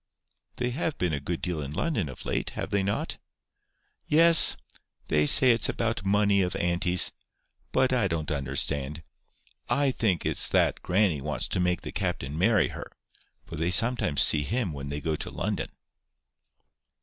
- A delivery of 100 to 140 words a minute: No, average, 165 wpm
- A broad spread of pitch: Yes, wide, 7.2 semitones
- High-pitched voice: No, very low, 90 Hz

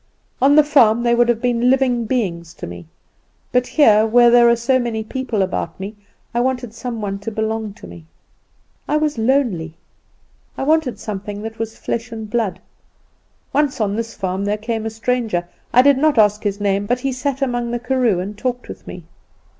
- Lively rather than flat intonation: No, average, 3.3 semitones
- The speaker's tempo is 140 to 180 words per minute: No, average, 195 wpm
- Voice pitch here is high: Yes, high, 230 Hz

